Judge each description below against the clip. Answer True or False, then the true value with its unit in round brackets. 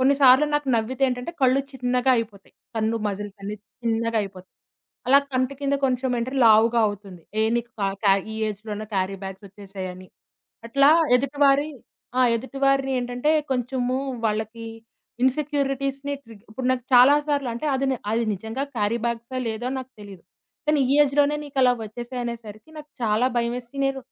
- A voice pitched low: False (245 Hz)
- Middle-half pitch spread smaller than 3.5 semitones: False (3.8 semitones)